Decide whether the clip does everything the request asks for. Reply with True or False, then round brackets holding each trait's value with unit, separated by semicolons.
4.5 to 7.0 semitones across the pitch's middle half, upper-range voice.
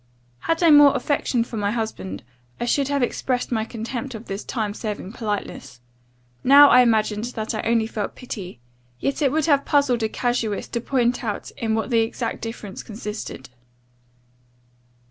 False (3.1 semitones; 230 Hz)